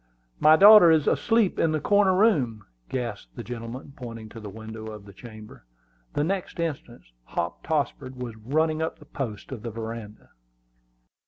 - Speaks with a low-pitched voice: Yes, low, 125 Hz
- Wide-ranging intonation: Yes, wide, 6.3 semitones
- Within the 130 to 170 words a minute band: Yes, average, 165 wpm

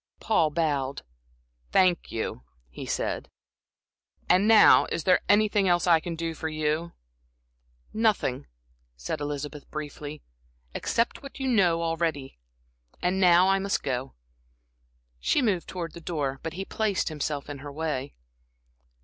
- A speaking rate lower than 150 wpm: Yes, slow, 135 wpm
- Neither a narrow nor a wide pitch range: Yes, average, 4.2 semitones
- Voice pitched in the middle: Yes, medium, 165 Hz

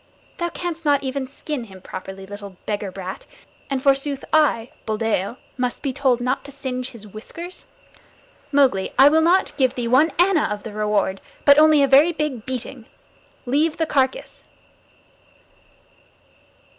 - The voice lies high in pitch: Yes, very high, 260 Hz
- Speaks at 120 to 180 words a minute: Yes, average, 150 wpm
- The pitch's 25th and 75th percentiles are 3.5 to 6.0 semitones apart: Yes, average, 5.3 semitones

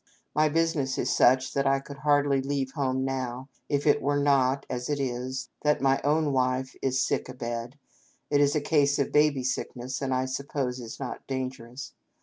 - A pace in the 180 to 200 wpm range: Yes, average, 190 wpm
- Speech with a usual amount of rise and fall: No, narrow, 1.9 semitones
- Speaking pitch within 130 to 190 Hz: Yes, low, 135 Hz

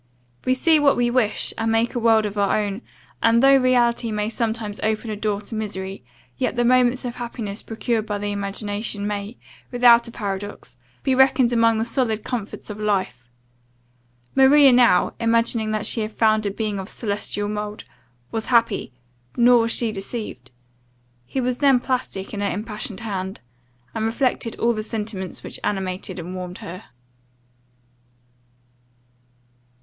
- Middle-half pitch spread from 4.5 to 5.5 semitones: No, average, 2.8 semitones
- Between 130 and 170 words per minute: Yes, average, 160 wpm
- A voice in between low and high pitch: No, high, 220 Hz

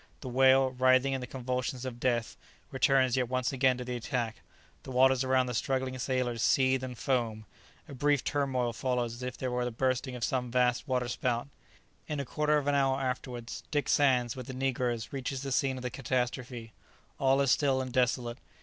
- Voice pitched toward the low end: Yes, low, 130 Hz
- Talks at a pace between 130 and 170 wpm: No, average, 195 wpm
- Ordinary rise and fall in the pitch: No, narrow, 1.4 semitones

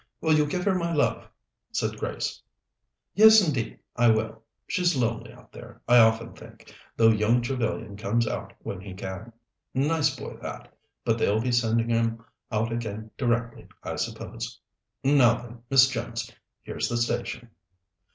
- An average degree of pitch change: Yes, average, 3.0 semitones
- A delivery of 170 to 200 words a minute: No, average, 155 wpm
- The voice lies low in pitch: Yes, low, 120 Hz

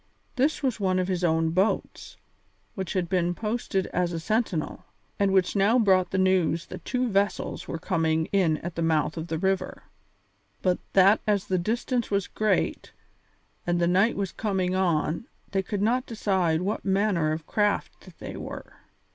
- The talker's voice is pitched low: No, high, 190 Hz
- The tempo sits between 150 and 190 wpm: Yes, average, 170 wpm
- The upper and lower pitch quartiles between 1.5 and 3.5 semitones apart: Yes, average, 3.2 semitones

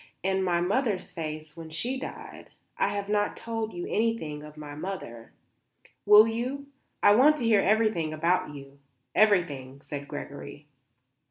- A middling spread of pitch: No, wide, 6.3 semitones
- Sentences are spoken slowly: No, average, 150 wpm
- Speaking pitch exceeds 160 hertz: Yes, medium, 185 Hz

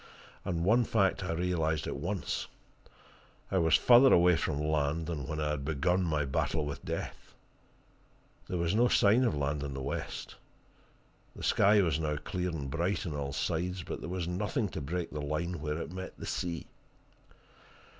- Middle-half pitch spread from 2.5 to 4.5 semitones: Yes, average, 3.4 semitones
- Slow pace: No, average, 180 wpm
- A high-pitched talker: No, very low, 85 Hz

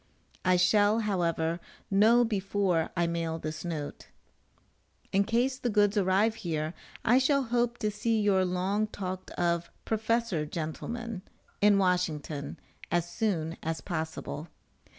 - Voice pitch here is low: No, high, 190 Hz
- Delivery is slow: Yes, slow, 130 wpm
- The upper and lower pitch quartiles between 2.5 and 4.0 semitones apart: No, average, 4.6 semitones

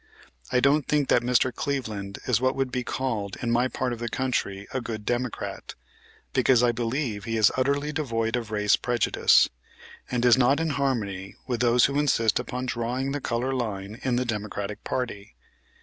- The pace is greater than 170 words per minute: Yes, average, 180 wpm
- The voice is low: Yes, low, 120 Hz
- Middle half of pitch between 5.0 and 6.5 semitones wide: No, average, 2.8 semitones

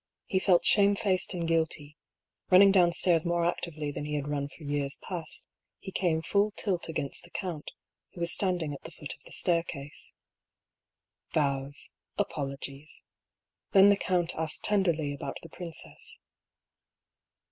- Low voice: No, medium, 165 Hz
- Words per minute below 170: Yes, average, 145 wpm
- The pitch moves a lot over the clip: No, average, 3.9 semitones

